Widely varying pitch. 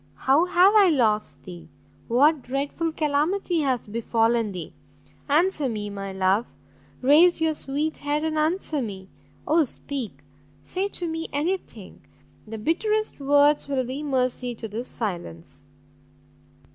Yes: wide, 6.1 semitones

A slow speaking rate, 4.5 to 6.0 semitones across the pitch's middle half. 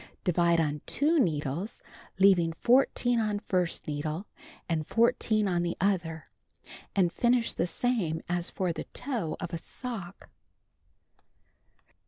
Yes: slow, 125 wpm; average, 5.2 semitones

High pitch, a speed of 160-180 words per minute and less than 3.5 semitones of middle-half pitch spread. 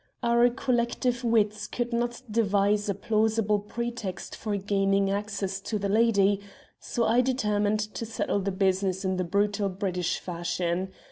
No: high, 205 Hz; average, 145 wpm; average, 2.9 semitones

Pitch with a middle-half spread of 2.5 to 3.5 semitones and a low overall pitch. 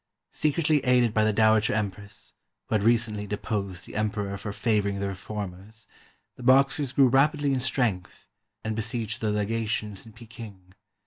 Yes: average, 2.9 semitones; low, 110 Hz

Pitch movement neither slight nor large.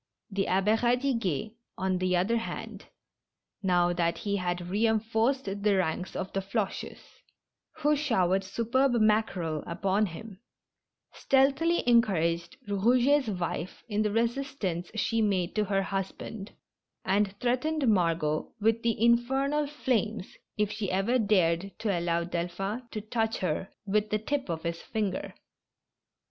Yes: average, 4.2 semitones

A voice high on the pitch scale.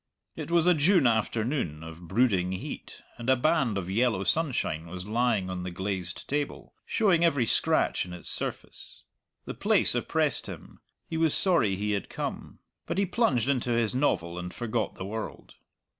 No: low, 115 Hz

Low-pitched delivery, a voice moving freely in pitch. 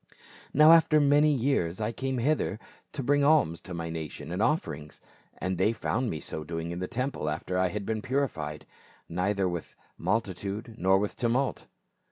Yes: low, 105 Hz; wide, 7.7 semitones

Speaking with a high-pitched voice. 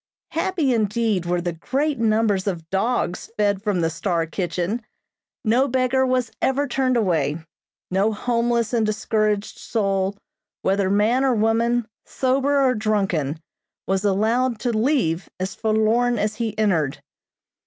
Yes: high, 215 Hz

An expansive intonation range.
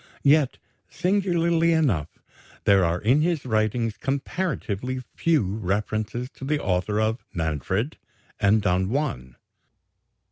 Yes: wide, 7.5 semitones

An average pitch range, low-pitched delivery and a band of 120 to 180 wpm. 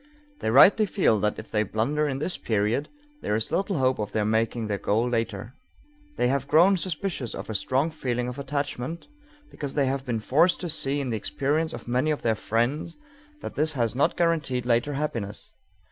No: average, 5.0 semitones; low, 130 Hz; average, 195 wpm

